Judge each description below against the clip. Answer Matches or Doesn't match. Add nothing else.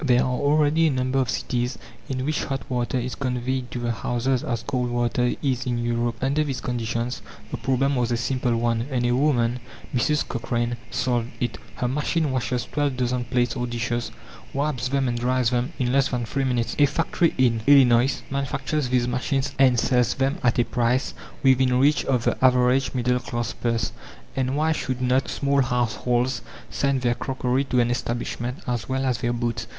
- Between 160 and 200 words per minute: Matches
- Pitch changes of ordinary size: Doesn't match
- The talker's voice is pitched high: Doesn't match